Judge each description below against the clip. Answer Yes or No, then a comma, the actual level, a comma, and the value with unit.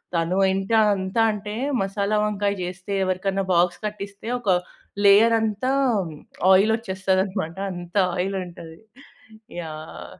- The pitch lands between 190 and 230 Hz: Yes, high, 195 Hz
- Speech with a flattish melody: Yes, narrow, 2.3 semitones